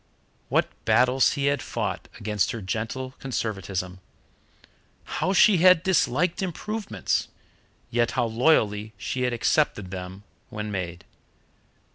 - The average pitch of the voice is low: Yes, low, 120 Hz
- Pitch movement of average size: No, wide, 6.8 semitones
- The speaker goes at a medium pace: No, slow, 115 wpm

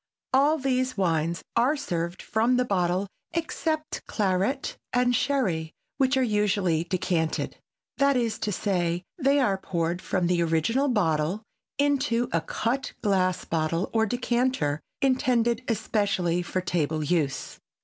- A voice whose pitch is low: No, high, 205 Hz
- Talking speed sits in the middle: No, slow, 130 wpm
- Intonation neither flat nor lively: No, wide, 6.8 semitones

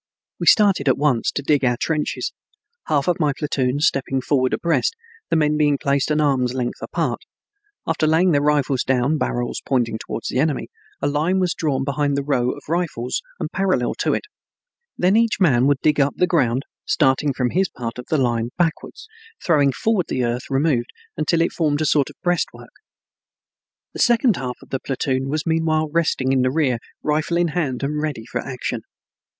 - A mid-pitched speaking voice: Yes, medium, 145 Hz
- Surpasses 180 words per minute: Yes, average, 190 wpm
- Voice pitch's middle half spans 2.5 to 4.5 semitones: Yes, average, 3.7 semitones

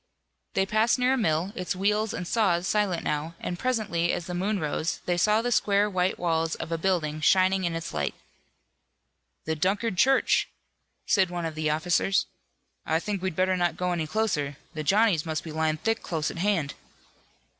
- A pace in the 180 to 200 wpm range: Yes, average, 190 wpm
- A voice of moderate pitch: Yes, medium, 180 Hz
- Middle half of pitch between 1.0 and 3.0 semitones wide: No, average, 4.0 semitones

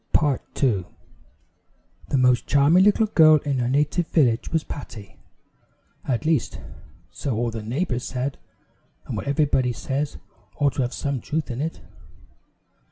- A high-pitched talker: No, medium, 140 Hz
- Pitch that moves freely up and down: No, average, 3.6 semitones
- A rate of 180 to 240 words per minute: No, average, 150 wpm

